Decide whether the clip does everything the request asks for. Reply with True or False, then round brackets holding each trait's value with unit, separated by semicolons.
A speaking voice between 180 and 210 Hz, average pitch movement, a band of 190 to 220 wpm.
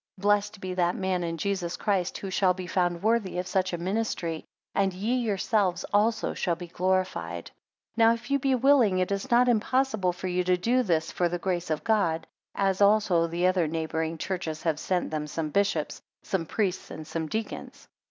True (185 Hz; 3.3 semitones; 200 wpm)